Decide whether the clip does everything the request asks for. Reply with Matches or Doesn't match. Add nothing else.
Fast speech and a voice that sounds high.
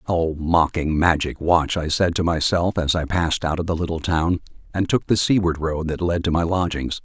Doesn't match